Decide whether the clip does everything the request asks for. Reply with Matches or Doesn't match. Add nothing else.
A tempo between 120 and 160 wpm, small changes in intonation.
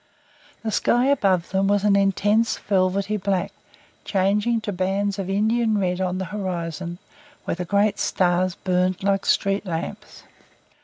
Matches